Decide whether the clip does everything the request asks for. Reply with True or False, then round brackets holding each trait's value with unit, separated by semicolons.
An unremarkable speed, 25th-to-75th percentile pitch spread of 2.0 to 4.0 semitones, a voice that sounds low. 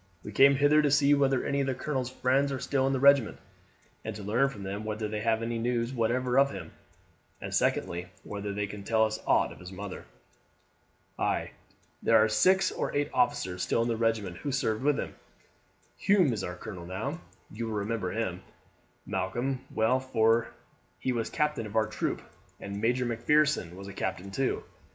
False (190 wpm; 4.8 semitones; 115 Hz)